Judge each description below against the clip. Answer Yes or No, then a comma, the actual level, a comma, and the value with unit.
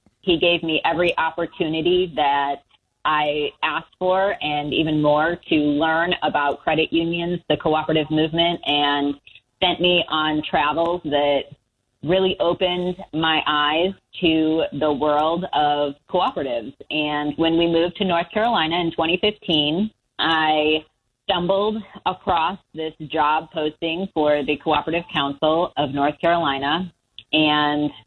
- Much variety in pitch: No, narrow, 2.6 semitones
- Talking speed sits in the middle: No, slow, 125 wpm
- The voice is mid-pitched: Yes, medium, 155 Hz